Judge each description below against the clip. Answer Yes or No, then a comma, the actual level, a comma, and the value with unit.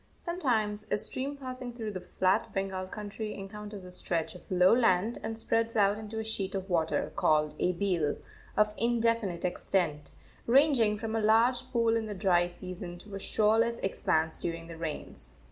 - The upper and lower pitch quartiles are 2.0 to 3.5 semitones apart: No, average, 3.9 semitones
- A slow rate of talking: No, average, 175 wpm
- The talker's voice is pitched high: Yes, high, 210 Hz